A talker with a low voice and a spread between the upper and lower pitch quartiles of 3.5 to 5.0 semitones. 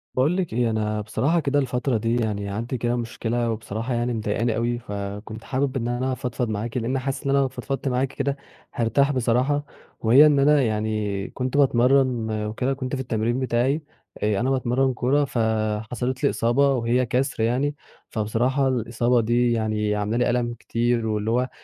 No: low, 120 Hz; average, 2.8 semitones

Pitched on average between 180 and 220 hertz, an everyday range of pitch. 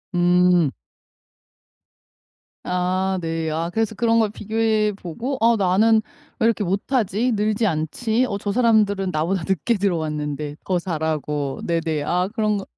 Yes: high, 190 Hz; average, 4.9 semitones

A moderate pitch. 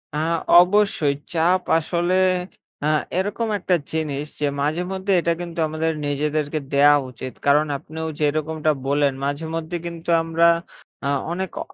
Yes: medium, 160 Hz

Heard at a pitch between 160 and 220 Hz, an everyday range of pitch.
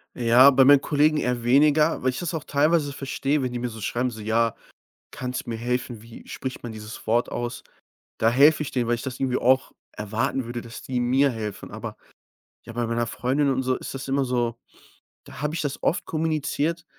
No: low, 125 Hz; average, 3.1 semitones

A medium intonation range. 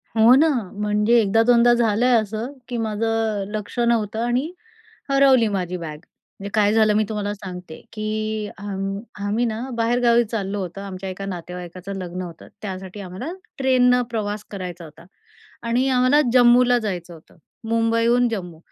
Yes: average, 3.6 semitones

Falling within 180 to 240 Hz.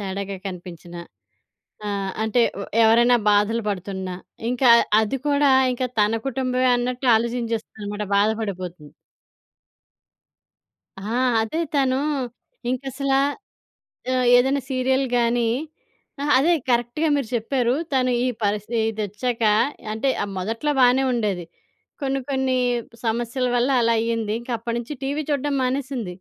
Yes: high, 235 Hz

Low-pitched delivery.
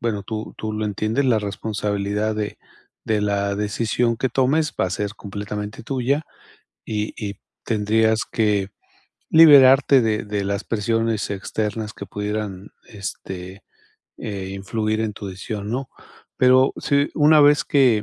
Yes: low, 110 Hz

